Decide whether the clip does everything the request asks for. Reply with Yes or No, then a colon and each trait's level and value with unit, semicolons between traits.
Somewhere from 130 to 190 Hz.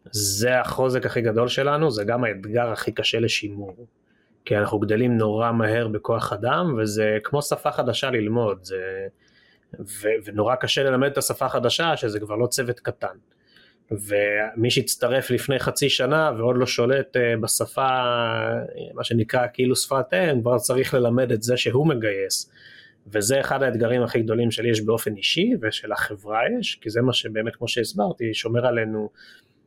No: low, 120 Hz